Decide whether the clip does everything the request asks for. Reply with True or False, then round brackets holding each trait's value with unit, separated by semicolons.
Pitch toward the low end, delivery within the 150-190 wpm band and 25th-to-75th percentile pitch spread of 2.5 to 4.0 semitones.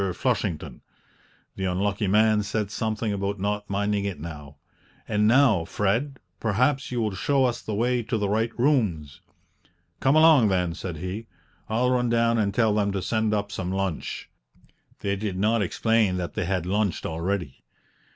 True (105 Hz; 165 wpm; 3.3 semitones)